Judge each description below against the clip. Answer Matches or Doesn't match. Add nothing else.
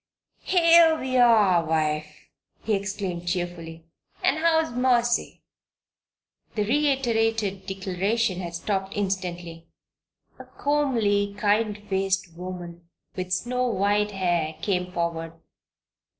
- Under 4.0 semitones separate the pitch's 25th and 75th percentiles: Doesn't match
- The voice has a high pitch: Matches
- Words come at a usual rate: Doesn't match